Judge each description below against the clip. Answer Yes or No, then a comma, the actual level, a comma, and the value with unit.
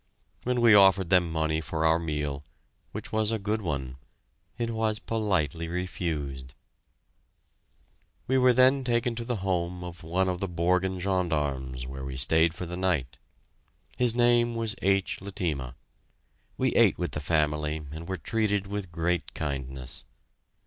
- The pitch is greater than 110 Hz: No, very low, 90 Hz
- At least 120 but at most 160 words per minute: Yes, average, 150 wpm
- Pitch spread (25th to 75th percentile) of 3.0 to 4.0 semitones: No, wide, 5.4 semitones